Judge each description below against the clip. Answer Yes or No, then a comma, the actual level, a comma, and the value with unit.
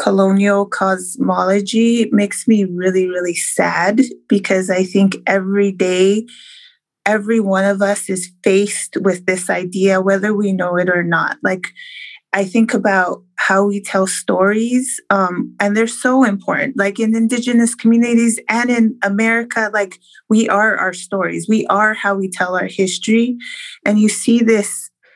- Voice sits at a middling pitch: No, high, 205 Hz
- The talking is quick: No, average, 150 wpm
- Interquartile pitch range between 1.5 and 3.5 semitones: Yes, average, 3.0 semitones